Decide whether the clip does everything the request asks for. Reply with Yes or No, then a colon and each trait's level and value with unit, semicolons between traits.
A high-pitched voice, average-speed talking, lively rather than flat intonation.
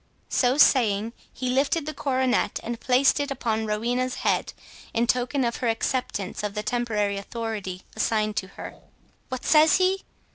No: high, 240 Hz; average, 155 wpm; average, 3.5 semitones